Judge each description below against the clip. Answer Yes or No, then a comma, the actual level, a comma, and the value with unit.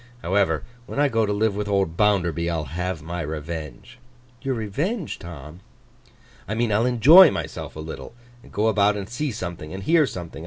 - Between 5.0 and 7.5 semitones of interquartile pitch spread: Yes, average, 5.3 semitones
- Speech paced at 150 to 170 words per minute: No, average, 185 wpm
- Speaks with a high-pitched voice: No, low, 100 Hz